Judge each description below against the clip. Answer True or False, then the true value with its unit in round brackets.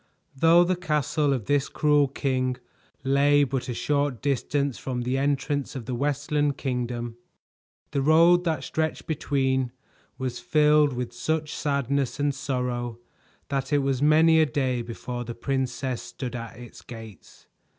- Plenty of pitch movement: False (2.8 semitones)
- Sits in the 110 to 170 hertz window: True (140 Hz)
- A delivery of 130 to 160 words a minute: True (150 wpm)